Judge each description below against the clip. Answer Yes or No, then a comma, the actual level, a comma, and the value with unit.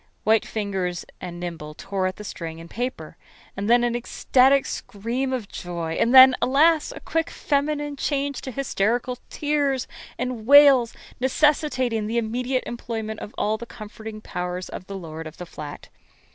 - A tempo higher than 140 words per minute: Yes, average, 160 wpm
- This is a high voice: Yes, high, 230 Hz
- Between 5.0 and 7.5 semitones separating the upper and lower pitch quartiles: Yes, wide, 5.4 semitones